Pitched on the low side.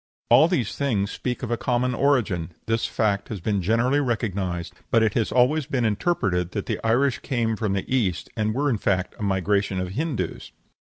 Yes: low, 110 Hz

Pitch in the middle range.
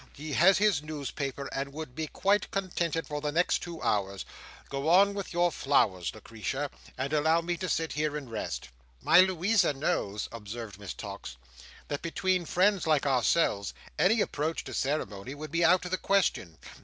Yes: medium, 155 Hz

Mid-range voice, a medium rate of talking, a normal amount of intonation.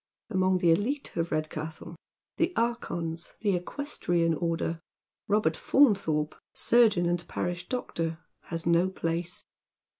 No: medium, 175 Hz; slow, 130 wpm; average, 3.8 semitones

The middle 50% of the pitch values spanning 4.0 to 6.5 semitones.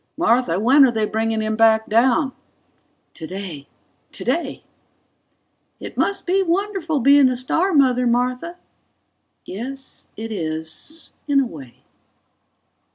Yes: average, 4.9 semitones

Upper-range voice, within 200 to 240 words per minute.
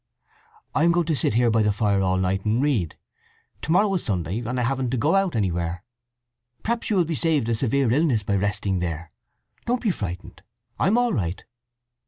No: low, 115 Hz; fast, 205 wpm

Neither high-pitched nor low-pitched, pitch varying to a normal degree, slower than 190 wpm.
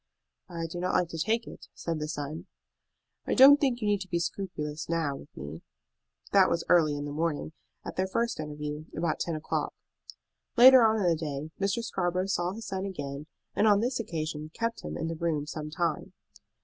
No: medium, 170 Hz; average, 4.6 semitones; average, 200 wpm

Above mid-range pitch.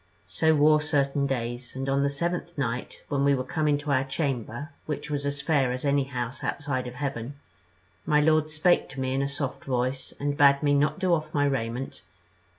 No: medium, 140 Hz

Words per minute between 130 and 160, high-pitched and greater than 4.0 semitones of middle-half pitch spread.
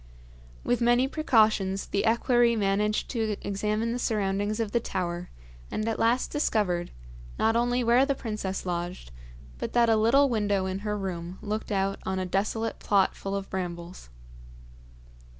No: average, 155 wpm; high, 210 Hz; average, 3.3 semitones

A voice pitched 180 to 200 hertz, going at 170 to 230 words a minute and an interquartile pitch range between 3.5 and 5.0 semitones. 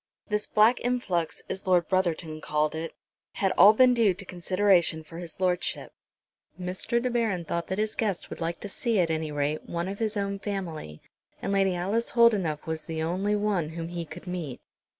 Yes: medium, 185 Hz; average, 190 wpm; average, 3.9 semitones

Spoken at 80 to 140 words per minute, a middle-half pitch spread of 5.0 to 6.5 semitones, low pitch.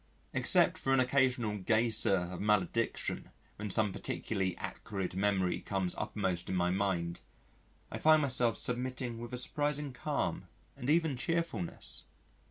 Yes: slow, 135 wpm; average, 5.3 semitones; low, 110 Hz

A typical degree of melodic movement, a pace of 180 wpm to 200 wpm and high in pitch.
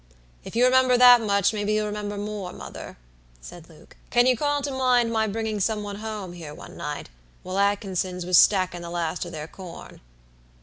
Yes: average, 4.0 semitones; average, 190 wpm; high, 205 Hz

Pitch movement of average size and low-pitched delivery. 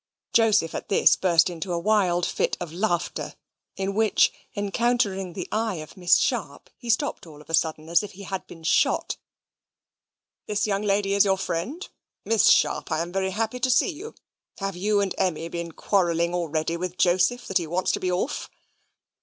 No: average, 3.6 semitones; high, 190 Hz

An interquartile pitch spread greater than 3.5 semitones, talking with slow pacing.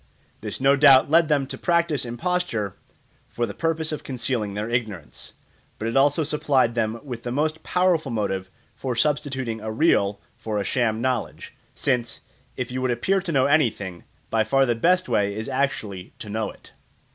No: average, 4.9 semitones; average, 180 wpm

